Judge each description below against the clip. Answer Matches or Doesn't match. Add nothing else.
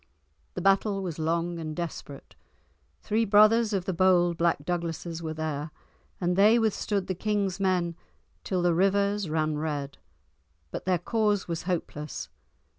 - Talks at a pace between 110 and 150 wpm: Matches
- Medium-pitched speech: Matches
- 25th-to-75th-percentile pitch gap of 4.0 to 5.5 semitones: Doesn't match